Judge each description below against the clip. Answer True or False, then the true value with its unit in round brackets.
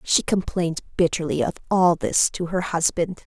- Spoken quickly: False (160 wpm)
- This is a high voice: False (175 Hz)